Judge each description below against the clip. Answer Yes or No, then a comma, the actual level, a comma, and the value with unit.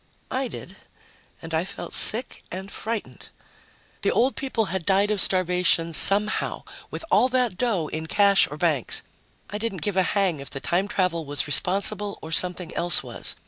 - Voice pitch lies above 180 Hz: Yes, high, 190 Hz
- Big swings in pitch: No, average, 3.8 semitones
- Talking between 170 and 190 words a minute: Yes, average, 175 wpm